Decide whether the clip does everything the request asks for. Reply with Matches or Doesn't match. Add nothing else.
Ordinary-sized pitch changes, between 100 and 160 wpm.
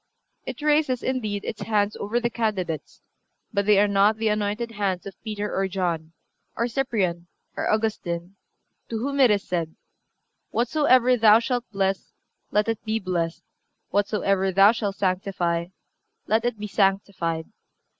Matches